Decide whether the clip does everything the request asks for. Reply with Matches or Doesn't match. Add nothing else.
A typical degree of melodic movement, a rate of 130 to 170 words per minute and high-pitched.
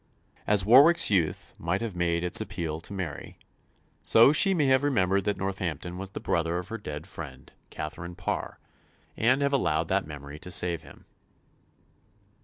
Doesn't match